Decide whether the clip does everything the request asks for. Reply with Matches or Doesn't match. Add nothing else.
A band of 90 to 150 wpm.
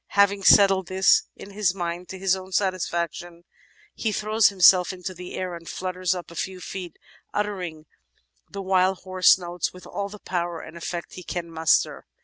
Doesn't match